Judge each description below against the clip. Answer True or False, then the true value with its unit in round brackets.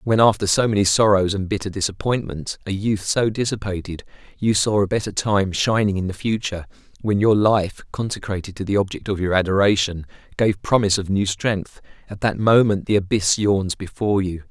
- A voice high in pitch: False (100 Hz)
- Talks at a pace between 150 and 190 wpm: True (180 wpm)